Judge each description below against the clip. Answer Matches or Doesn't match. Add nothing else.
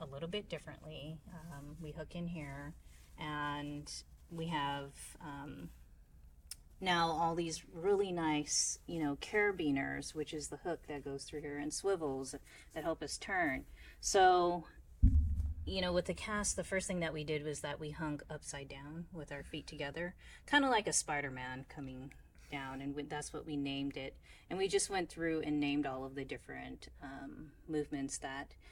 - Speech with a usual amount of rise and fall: Matches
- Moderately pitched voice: Matches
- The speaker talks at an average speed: Matches